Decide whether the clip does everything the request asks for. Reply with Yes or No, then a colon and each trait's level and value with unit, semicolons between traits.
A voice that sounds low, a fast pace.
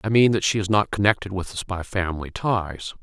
Yes: low, 100 Hz; fast, 240 wpm